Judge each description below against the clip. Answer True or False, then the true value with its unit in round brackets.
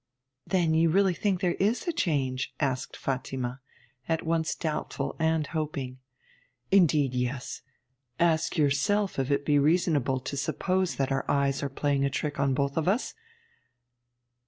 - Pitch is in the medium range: True (150 Hz)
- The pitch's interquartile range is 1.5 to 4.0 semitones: True (3.7 semitones)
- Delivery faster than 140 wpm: True (150 wpm)